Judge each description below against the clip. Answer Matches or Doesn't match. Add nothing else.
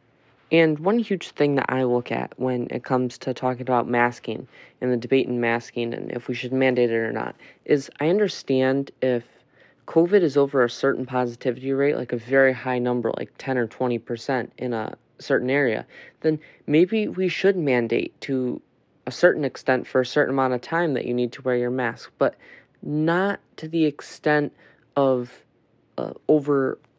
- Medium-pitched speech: Doesn't match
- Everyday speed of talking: Matches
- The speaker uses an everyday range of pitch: Matches